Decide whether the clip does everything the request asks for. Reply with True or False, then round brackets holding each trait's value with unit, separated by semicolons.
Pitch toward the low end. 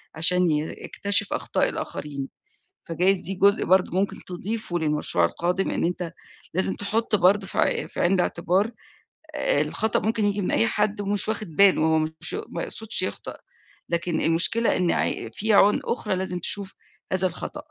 False (185 Hz)